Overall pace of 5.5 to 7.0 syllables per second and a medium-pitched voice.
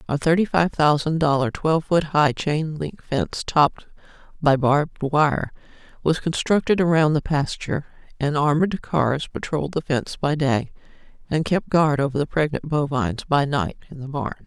No: 5.1 syllables/s; medium, 145 Hz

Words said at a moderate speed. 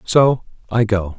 Yes: average, 150 wpm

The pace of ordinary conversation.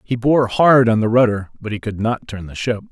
No: fast, 265 wpm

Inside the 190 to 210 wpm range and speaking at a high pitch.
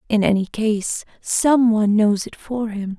No: average, 180 wpm; high, 215 Hz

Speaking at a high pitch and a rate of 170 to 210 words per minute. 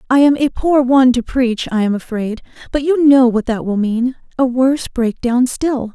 Yes: very high, 250 Hz; average, 200 wpm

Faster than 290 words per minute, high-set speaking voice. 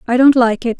Yes: fast, 305 wpm; high, 245 Hz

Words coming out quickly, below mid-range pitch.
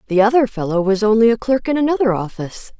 No: fast, 215 wpm; high, 220 Hz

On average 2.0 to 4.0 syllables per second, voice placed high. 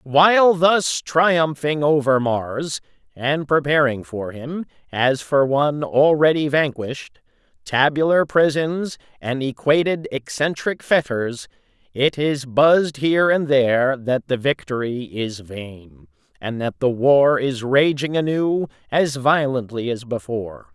No: 3.9 syllables/s; medium, 140 Hz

